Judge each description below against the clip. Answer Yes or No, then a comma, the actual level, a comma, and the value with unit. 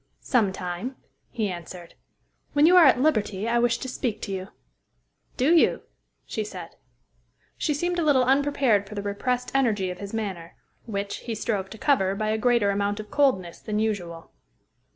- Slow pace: No, average, 175 wpm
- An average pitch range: Yes, average, 4.5 semitones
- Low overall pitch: No, high, 215 Hz